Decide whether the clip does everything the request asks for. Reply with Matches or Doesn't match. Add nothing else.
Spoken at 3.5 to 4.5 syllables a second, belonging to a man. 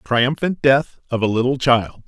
Matches